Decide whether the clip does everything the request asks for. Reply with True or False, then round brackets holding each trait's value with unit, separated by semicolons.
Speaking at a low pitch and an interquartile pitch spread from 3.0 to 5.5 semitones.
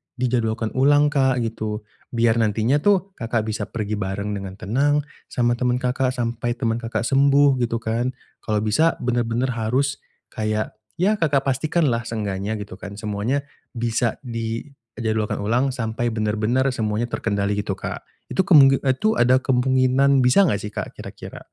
True (120 Hz; 3.4 semitones)